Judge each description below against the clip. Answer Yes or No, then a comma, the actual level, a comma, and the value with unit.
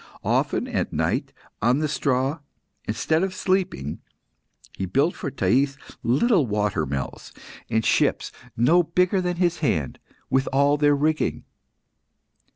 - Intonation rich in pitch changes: Yes, wide, 6.7 semitones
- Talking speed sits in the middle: No, slow, 130 wpm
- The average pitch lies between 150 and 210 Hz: No, medium, 140 Hz